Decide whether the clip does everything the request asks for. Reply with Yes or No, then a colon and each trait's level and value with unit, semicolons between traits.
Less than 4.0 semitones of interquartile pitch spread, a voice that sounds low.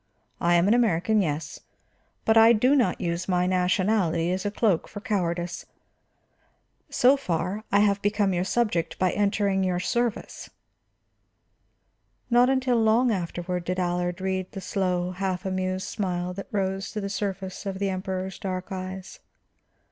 No: narrow, 2.5 semitones; high, 190 Hz